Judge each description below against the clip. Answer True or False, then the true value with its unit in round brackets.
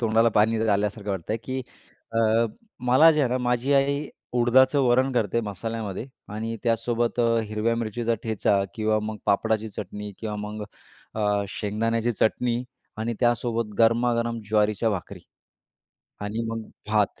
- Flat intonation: True (2.2 semitones)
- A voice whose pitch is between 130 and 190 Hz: False (115 Hz)